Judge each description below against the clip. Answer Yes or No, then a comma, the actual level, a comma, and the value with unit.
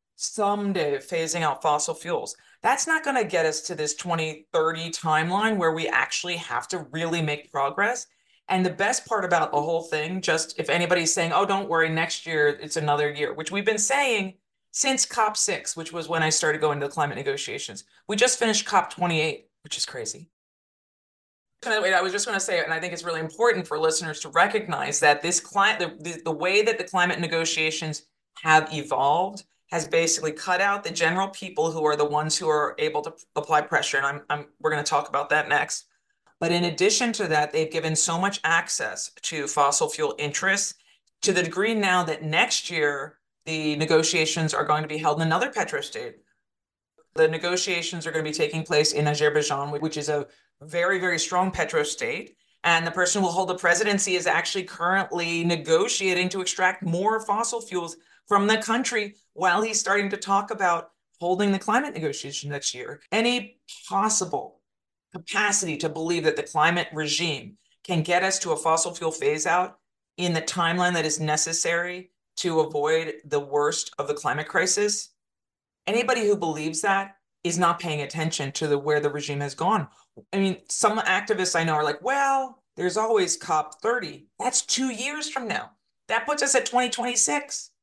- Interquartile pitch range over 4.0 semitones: Yes, average, 4.7 semitones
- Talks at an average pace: Yes, average, 190 wpm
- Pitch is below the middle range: No, medium, 175 Hz